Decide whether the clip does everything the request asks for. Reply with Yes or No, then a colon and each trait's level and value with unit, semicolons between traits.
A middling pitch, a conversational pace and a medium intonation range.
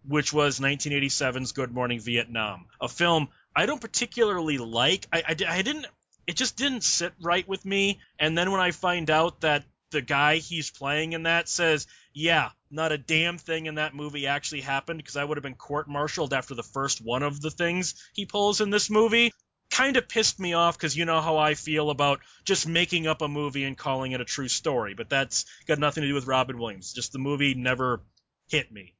No: medium, 150 Hz; fast, 215 wpm; average, 3.9 semitones